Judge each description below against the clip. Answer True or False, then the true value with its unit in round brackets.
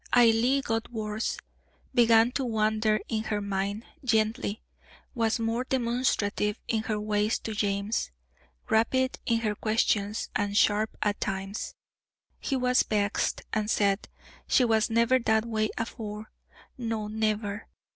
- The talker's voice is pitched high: True (220 Hz)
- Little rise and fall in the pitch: True (1.8 semitones)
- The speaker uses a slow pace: True (130 wpm)